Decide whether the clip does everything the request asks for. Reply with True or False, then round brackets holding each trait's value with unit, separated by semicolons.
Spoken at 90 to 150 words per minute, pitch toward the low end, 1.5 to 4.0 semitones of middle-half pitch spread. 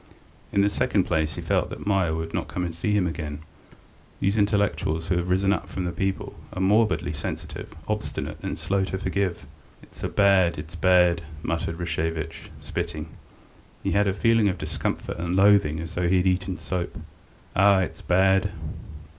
False (170 wpm; 90 Hz; 3.0 semitones)